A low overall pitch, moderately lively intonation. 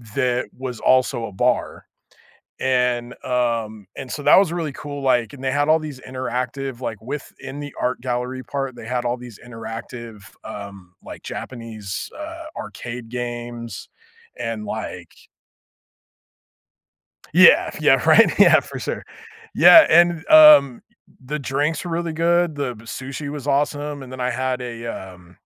Yes: low, 130 Hz; average, 3.6 semitones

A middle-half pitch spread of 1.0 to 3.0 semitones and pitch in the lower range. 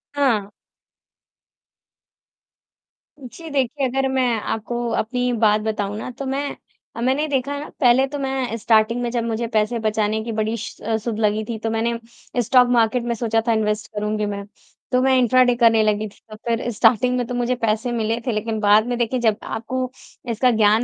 No: narrow, 2.6 semitones; high, 230 Hz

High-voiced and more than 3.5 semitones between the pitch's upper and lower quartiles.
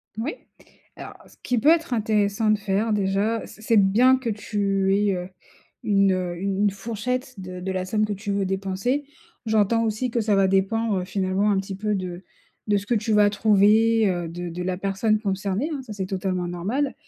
No: high, 205 Hz; narrow, 2.6 semitones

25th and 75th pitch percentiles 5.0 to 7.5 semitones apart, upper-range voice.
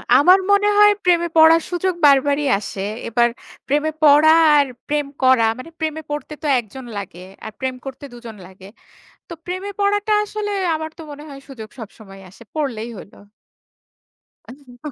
Yes: wide, 5.4 semitones; very high, 290 Hz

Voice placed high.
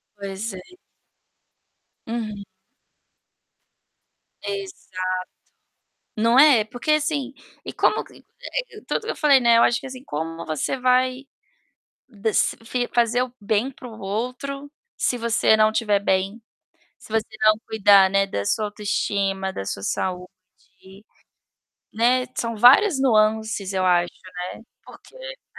Yes: high, 220 Hz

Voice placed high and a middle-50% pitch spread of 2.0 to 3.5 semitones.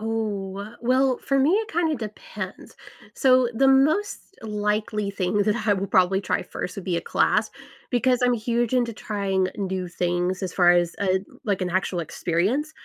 No: high, 210 Hz; average, 4.8 semitones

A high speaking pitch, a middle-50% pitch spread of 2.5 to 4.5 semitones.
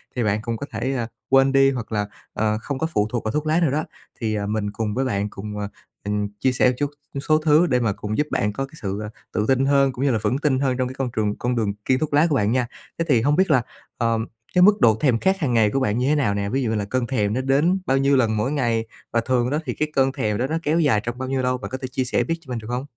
No: low, 125 Hz; average, 4.0 semitones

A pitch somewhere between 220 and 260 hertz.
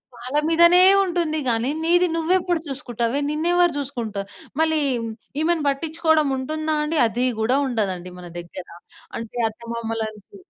No: very high, 285 Hz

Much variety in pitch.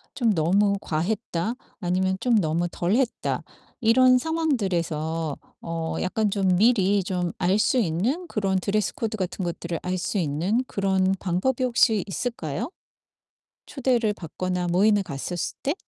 No: average, 4.4 semitones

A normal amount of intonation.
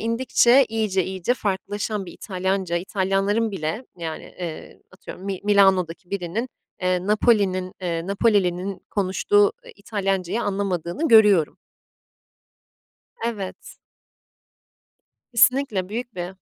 Yes: average, 3.1 semitones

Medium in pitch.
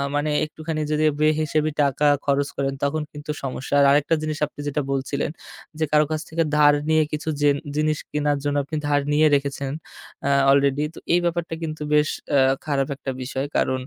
Yes: medium, 150 Hz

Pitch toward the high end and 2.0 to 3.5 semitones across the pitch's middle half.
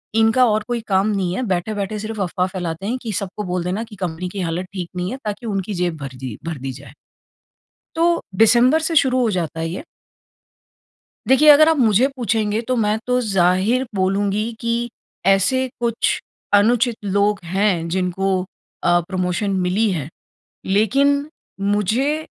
No: high, 205 Hz; average, 4.5 semitones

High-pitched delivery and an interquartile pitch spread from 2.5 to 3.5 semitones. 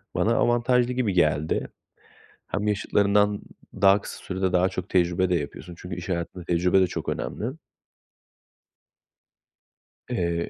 No: very low, 95 Hz; average, 2.9 semitones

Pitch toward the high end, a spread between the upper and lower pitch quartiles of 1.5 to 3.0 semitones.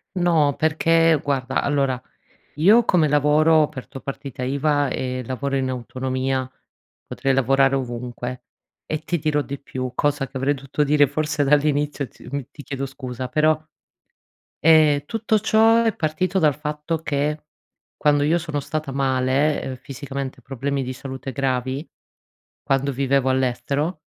No: medium, 140 Hz; narrow, 2.5 semitones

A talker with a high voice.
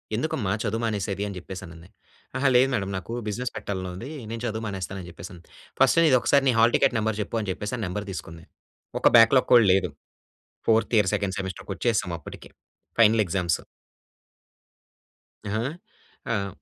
No: low, 105 Hz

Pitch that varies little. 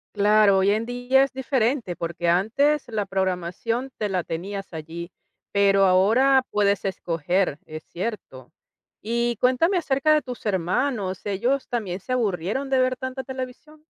No: wide, 5.6 semitones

